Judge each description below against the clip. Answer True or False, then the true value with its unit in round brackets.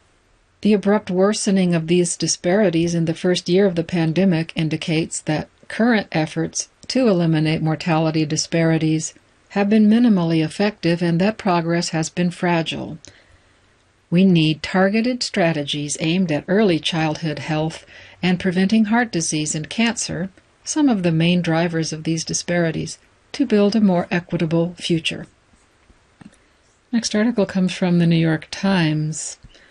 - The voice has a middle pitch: True (170 Hz)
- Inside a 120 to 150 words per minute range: True (135 wpm)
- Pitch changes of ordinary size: True (3.4 semitones)